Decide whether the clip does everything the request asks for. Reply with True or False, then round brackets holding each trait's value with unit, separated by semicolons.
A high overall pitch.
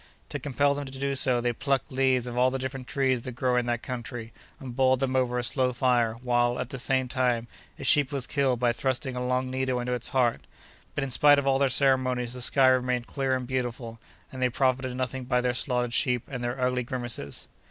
False (125 Hz)